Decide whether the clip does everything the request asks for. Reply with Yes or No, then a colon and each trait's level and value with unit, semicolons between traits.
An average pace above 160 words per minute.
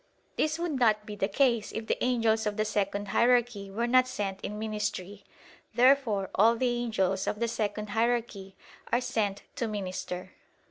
Yes: average, 170 wpm